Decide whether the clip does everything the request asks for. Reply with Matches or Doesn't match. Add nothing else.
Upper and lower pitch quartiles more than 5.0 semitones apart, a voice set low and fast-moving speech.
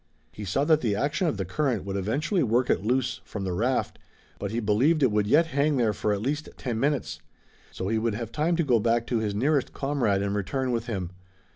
Matches